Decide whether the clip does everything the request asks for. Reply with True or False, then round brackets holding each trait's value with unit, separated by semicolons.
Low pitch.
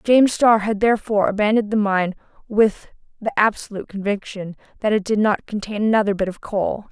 False (205 Hz)